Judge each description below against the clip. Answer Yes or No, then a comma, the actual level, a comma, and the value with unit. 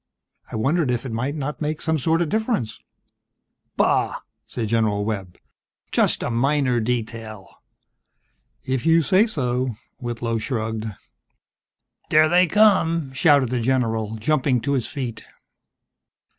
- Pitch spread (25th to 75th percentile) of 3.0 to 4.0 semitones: No, average, 5.3 semitones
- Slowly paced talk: Yes, slow, 130 wpm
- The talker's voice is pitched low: Yes, low, 130 Hz